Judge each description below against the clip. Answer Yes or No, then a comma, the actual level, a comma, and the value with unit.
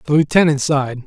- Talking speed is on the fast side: No, average, 170 wpm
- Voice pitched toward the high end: No, medium, 145 Hz